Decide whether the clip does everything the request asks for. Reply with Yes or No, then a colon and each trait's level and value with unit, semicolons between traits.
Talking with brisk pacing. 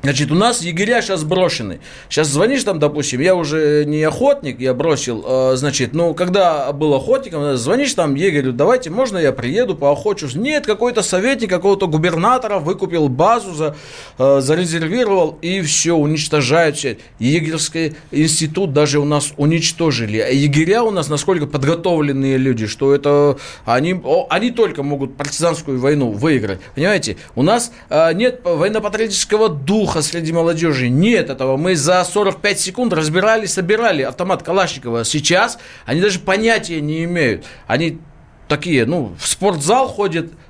No: average, 140 wpm